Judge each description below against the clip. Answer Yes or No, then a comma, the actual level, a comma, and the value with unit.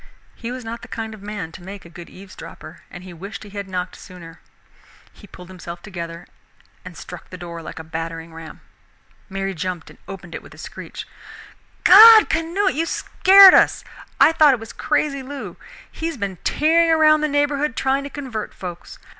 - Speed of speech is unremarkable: Yes, average, 195 wpm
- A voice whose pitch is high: Yes, high, 200 Hz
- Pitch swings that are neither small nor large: No, wide, 8.6 semitones